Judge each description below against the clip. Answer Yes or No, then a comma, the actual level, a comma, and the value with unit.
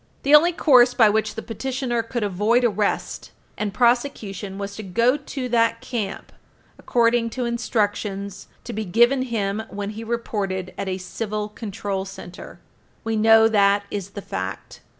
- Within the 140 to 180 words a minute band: Yes, average, 155 wpm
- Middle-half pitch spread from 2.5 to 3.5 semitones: Yes, average, 3.1 semitones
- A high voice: Yes, high, 220 Hz